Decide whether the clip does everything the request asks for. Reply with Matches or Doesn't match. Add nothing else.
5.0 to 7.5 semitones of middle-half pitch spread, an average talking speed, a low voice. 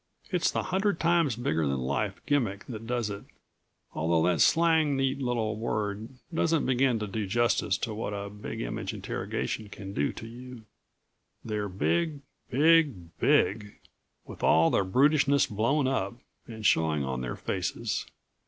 Matches